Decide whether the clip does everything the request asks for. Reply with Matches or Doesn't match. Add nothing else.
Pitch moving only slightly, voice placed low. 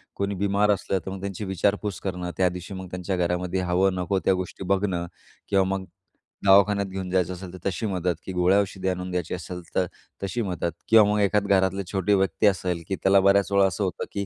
Matches